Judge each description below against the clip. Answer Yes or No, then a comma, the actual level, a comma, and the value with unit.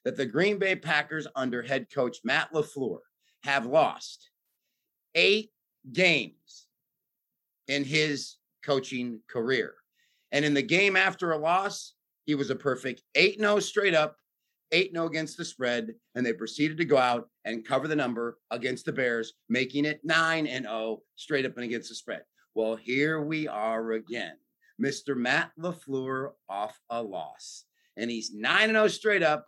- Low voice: No, medium, 150 Hz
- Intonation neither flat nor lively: No, wide, 6.1 semitones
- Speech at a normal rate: Yes, average, 165 wpm